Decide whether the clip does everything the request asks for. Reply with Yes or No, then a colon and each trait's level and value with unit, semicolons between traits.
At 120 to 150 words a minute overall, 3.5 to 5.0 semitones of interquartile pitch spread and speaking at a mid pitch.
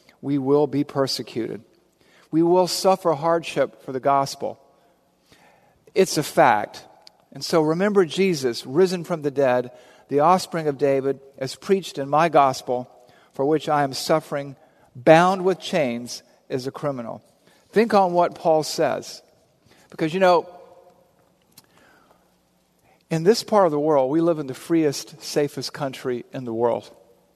Yes: average, 145 wpm; average, 4.3 semitones; medium, 155 Hz